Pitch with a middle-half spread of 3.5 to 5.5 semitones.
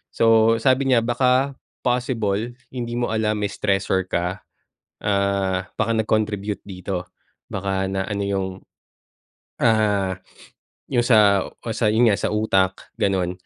No: average, 3.0 semitones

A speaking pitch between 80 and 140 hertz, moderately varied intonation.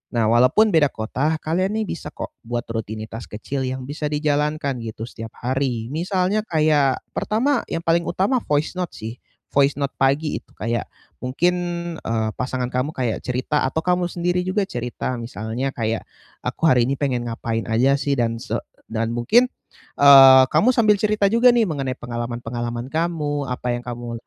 No: low, 135 Hz; wide, 5.7 semitones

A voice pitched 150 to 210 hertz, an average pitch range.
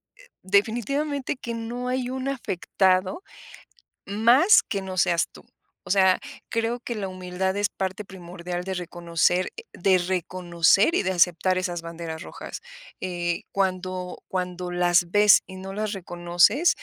Yes: medium, 185 Hz; average, 3.4 semitones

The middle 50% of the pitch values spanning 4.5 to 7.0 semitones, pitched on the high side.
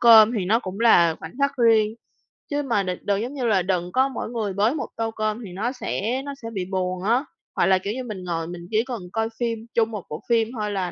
No: average, 3.9 semitones; high, 215 Hz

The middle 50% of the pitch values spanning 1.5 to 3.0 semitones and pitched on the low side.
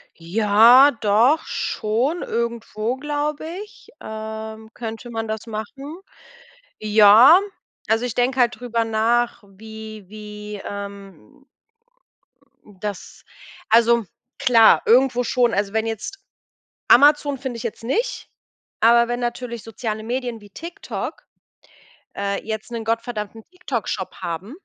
No: narrow, 2.5 semitones; high, 225 Hz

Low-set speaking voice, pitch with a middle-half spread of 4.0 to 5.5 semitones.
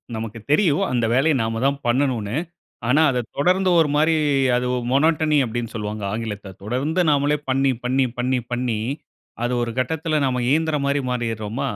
Yes: low, 130 Hz; average, 4.3 semitones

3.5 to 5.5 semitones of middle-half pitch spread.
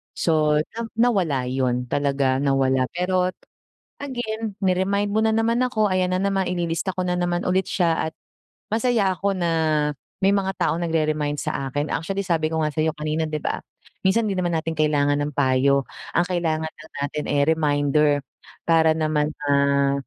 Yes: average, 4.6 semitones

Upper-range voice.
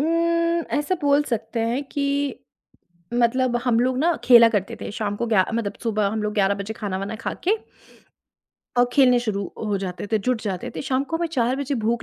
Yes: high, 235 Hz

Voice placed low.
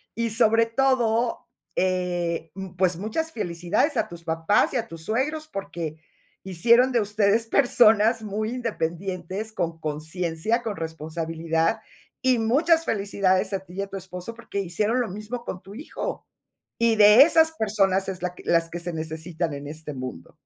No: high, 195 Hz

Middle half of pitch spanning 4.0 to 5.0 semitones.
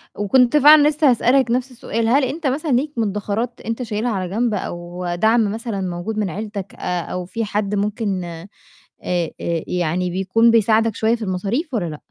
Yes: average, 4.4 semitones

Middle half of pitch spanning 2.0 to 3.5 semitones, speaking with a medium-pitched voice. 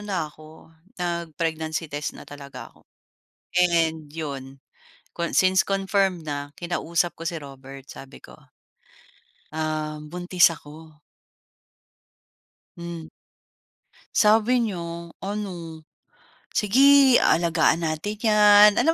No: average, 4.0 semitones; medium, 170 Hz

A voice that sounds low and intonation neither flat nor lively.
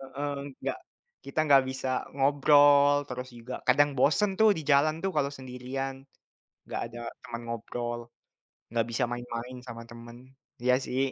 Yes: low, 130 Hz; average, 3.0 semitones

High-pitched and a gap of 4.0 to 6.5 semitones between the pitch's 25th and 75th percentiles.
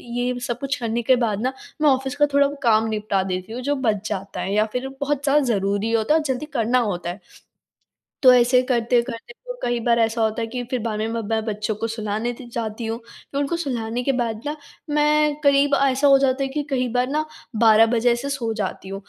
No: high, 240 Hz; average, 3.6 semitones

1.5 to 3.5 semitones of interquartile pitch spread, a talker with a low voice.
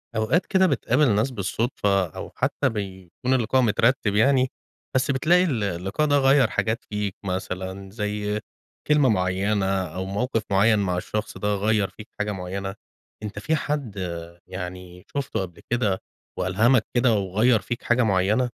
No: average, 4.7 semitones; low, 105 Hz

